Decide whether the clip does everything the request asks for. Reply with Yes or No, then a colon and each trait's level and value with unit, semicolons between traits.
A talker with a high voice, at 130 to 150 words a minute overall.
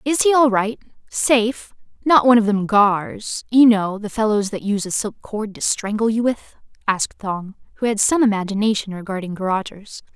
No: high, 215 Hz; average, 165 wpm